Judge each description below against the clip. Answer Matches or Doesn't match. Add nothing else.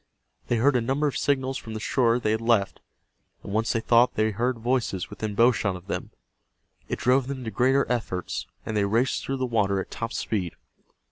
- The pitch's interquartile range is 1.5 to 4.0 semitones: Matches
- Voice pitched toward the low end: Matches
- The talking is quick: Matches